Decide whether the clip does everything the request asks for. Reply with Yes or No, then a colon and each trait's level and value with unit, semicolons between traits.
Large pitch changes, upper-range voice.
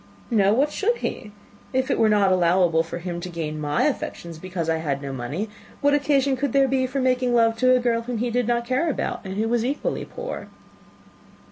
Yes: wide, 6.9 semitones; high, 230 Hz